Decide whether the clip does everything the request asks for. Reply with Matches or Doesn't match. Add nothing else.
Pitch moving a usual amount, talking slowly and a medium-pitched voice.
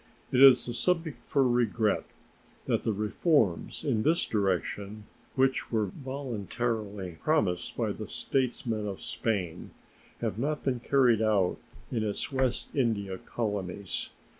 Doesn't match